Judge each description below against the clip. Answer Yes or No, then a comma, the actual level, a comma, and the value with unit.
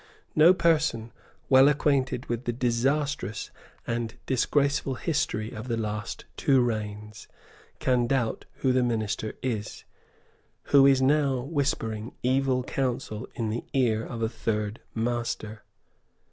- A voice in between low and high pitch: No, low, 120 Hz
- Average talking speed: No, slow, 125 wpm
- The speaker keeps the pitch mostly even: No, average, 3.5 semitones